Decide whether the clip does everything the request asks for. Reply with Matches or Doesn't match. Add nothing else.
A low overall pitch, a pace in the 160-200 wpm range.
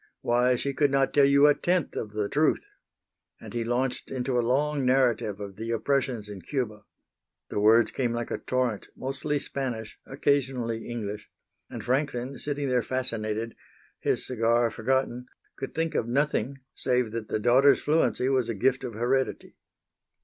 Matches